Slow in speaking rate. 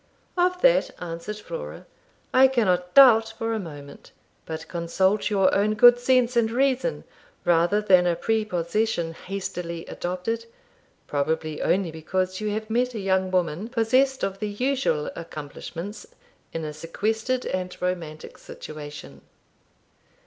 Yes: slow, 130 wpm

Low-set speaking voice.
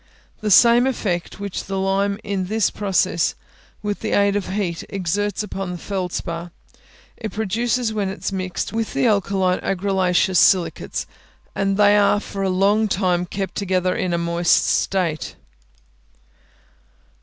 No: high, 195 Hz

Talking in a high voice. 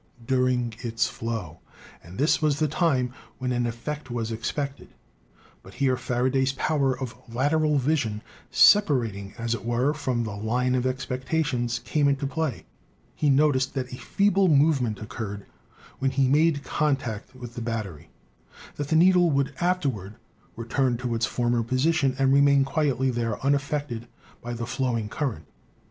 No: low, 130 Hz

